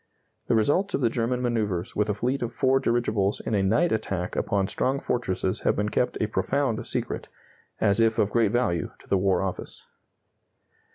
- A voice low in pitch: Yes, low, 110 Hz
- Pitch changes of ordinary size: Yes, average, 4.0 semitones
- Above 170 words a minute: Yes, average, 185 wpm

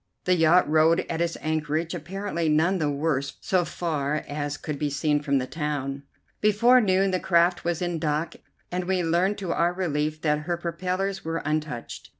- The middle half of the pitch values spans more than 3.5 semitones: No, average, 3.2 semitones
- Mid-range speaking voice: Yes, medium, 165 Hz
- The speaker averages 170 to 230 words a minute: Yes, average, 180 wpm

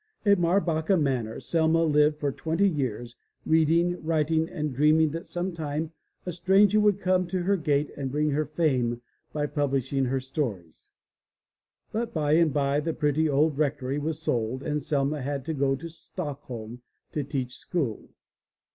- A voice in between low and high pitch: Yes, medium, 150 Hz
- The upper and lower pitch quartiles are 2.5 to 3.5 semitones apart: Yes, average, 3.2 semitones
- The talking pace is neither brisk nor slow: Yes, average, 155 wpm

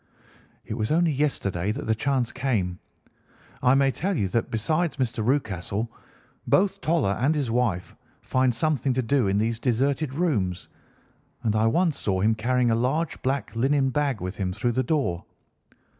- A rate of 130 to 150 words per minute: No, average, 170 wpm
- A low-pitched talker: Yes, low, 125 Hz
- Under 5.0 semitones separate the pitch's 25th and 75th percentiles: Yes, average, 4.6 semitones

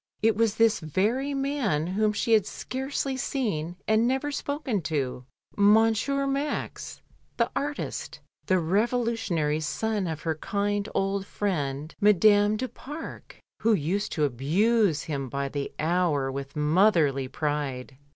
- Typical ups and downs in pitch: No, wide, 7.0 semitones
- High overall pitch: Yes, high, 200 Hz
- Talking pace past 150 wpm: No, slow, 135 wpm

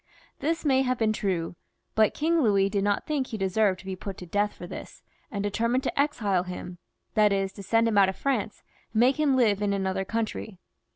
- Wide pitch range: No, average, 4.1 semitones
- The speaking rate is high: Yes, fast, 220 wpm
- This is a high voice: Yes, high, 210 Hz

